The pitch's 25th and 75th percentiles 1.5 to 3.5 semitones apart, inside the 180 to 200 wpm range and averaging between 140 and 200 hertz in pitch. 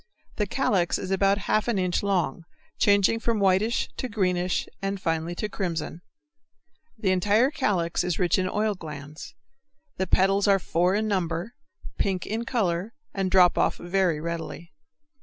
No: average, 3.0 semitones; average, 155 wpm; high, 190 Hz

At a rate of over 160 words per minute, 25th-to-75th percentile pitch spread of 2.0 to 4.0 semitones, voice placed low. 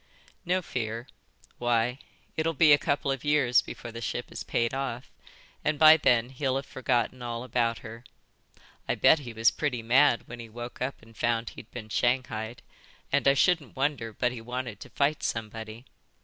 Yes: average, 180 wpm; average, 2.9 semitones; low, 125 Hz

